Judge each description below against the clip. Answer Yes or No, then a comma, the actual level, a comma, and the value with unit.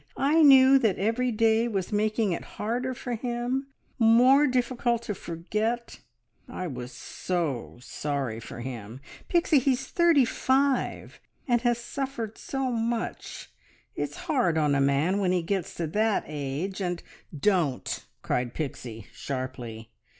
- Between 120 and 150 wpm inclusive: Yes, average, 145 wpm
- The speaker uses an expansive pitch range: Yes, wide, 8.8 semitones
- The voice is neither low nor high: No, high, 215 Hz